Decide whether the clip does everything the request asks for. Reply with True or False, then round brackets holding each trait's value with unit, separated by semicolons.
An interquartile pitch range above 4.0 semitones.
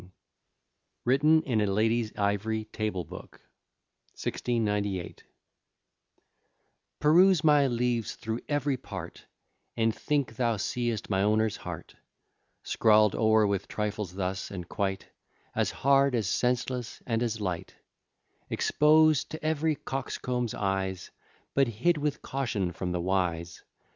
True (5.0 semitones)